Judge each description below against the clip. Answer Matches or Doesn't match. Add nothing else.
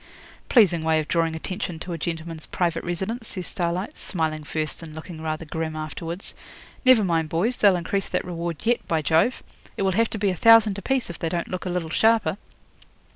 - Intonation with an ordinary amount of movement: Matches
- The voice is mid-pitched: Matches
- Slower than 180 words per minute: Doesn't match